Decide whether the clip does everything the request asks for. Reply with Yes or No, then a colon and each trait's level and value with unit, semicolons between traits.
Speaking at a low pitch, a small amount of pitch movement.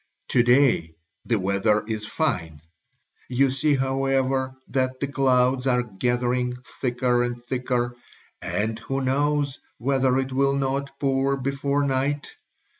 Yes: low, 130 Hz; narrow, 2.0 semitones